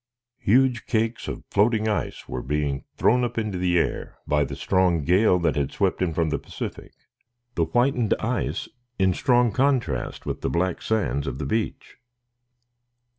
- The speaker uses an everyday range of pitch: No, wide, 6.0 semitones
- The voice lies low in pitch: Yes, very low, 95 Hz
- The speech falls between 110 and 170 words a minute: Yes, average, 160 wpm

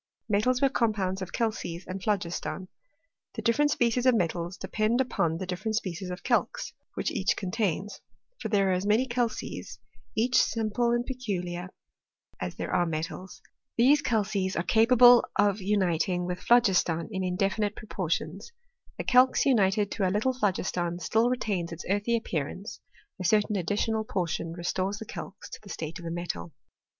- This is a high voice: Yes, high, 200 Hz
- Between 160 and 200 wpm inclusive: Yes, average, 165 wpm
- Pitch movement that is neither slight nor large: Yes, average, 4.1 semitones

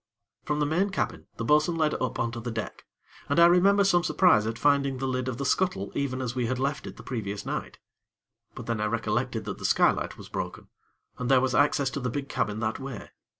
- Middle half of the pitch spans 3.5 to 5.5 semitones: Yes, average, 4.2 semitones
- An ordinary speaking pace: No, fast, 235 wpm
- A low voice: Yes, low, 130 Hz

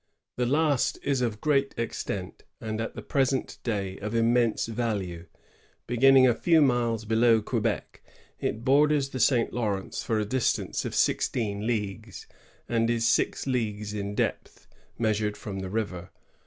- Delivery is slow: No, average, 150 wpm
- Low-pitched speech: Yes, low, 115 Hz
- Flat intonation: No, average, 3.1 semitones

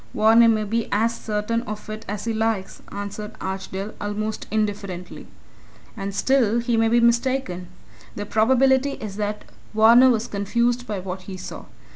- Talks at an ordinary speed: Yes, average, 155 wpm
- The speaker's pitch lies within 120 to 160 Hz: No, high, 215 Hz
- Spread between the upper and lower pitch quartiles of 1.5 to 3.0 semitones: Yes, narrow, 2.5 semitones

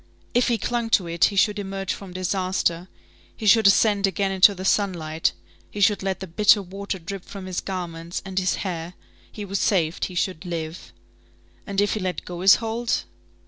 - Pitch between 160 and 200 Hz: Yes, high, 190 Hz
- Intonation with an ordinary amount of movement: No, narrow, 2.3 semitones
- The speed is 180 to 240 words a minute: Yes, average, 190 wpm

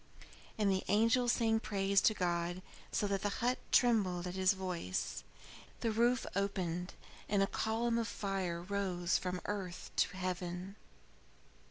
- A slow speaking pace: No, average, 145 wpm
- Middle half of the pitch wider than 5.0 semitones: No, average, 3.3 semitones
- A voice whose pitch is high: Yes, high, 195 Hz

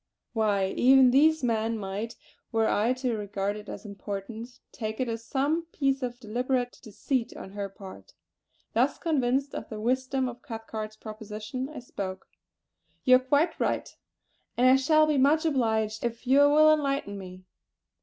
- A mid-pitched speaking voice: No, high, 240 Hz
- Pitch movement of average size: Yes, average, 4.0 semitones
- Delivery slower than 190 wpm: Yes, average, 170 wpm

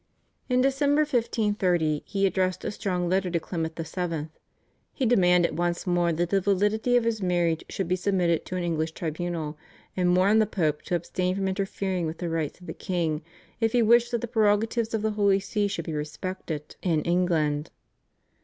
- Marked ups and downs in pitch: No, average, 3.7 semitones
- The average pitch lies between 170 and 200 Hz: Yes, medium, 185 Hz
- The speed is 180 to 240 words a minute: Yes, average, 185 wpm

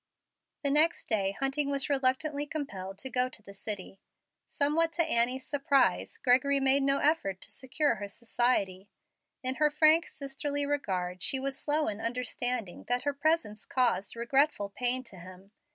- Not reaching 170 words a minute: Yes, average, 160 wpm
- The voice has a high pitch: Yes, very high, 260 Hz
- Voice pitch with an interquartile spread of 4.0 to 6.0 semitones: Yes, wide, 5.5 semitones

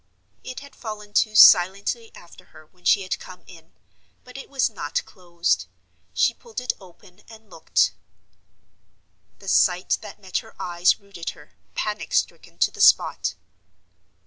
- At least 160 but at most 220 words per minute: No, average, 150 wpm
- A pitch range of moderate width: Yes, average, 3.8 semitones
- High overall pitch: Yes, high, 195 Hz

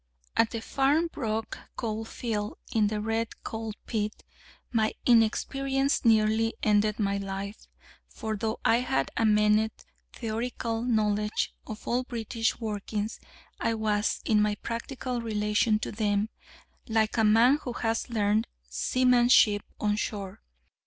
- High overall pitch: Yes, high, 220 Hz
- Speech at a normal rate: No, slow, 130 wpm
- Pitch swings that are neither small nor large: No, narrow, 1.7 semitones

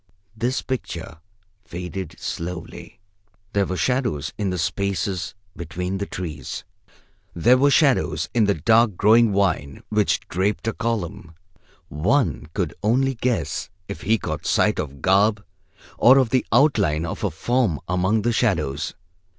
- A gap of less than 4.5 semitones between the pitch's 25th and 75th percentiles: No, average, 5.3 semitones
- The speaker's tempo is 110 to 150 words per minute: Yes, average, 140 wpm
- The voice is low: Yes, low, 100 Hz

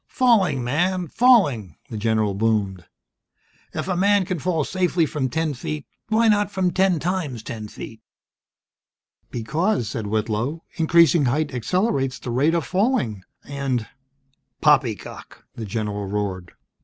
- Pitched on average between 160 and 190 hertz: No, medium, 140 Hz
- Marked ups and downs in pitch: Yes, wide, 8.5 semitones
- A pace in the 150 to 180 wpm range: No, slow, 135 wpm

